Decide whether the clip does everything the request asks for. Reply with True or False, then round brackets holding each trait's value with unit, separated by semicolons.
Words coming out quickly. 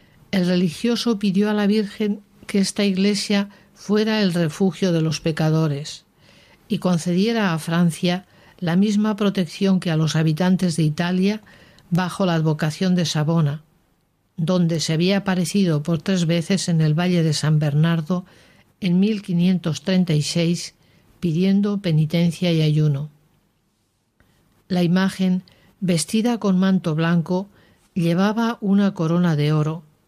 False (125 wpm)